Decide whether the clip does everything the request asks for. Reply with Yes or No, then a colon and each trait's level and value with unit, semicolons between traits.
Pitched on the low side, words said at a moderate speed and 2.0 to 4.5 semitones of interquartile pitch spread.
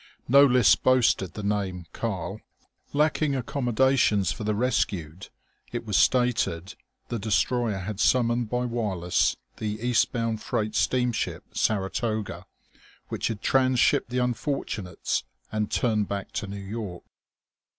No: low, 110 Hz; slow, 130 wpm; average, 3.6 semitones